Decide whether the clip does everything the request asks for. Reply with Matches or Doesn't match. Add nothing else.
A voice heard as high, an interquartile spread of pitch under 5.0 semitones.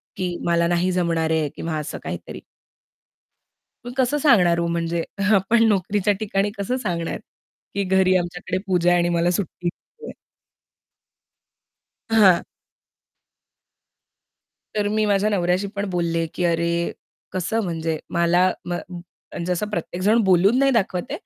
Doesn't match